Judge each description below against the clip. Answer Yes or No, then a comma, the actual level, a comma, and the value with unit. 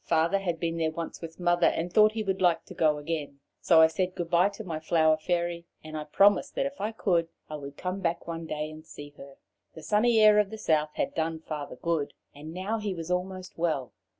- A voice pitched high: No, medium, 170 Hz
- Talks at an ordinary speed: No, fast, 230 wpm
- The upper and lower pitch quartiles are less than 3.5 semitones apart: Yes, average, 3.1 semitones